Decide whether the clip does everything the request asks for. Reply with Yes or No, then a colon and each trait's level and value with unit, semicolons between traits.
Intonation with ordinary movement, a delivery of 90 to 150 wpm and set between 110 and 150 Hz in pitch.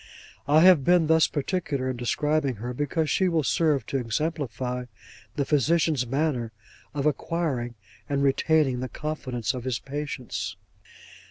Yes: average, 3.9 semitones; average, 140 wpm; medium, 140 Hz